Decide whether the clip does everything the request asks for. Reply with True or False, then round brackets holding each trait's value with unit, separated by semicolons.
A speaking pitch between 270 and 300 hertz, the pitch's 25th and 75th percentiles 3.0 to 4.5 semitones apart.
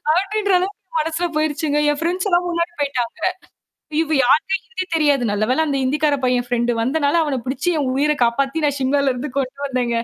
True (290 Hz; 4.0 semitones)